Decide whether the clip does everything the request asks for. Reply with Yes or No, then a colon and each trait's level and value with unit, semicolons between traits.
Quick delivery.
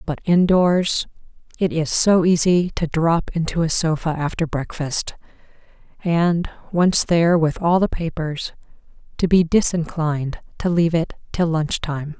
No: average, 145 wpm